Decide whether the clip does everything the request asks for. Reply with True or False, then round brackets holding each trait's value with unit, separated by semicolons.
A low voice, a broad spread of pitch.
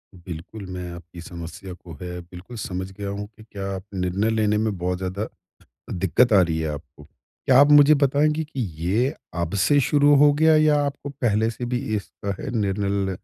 True (100 Hz; 6.0 semitones)